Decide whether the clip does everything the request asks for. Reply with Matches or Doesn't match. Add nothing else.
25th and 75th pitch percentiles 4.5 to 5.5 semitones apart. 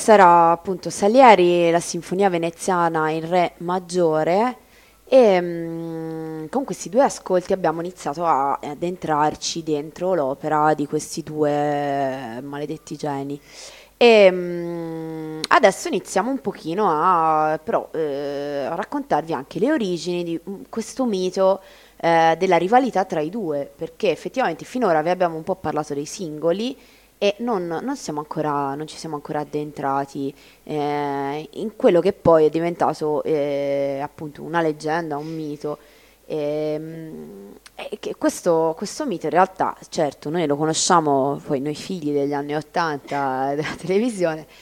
Doesn't match